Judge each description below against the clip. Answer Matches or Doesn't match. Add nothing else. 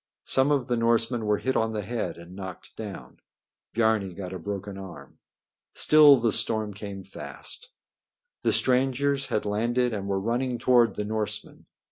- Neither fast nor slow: Matches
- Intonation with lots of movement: Doesn't match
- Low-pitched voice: Matches